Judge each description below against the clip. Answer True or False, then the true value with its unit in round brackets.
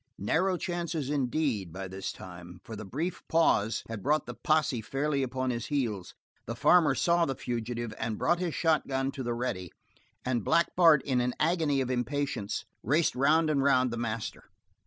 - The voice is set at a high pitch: False (130 Hz)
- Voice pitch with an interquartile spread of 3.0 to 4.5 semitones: False (5.0 semitones)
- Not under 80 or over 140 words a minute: False (180 wpm)